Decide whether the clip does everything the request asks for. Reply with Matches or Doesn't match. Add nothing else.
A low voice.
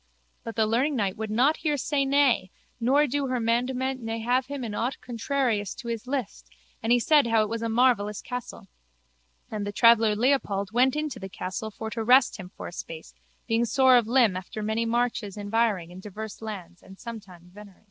Doesn't match